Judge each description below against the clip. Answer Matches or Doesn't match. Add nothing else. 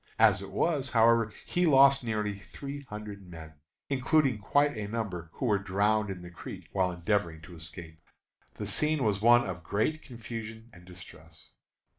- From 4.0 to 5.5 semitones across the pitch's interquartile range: Matches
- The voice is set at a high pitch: Doesn't match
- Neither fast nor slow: Matches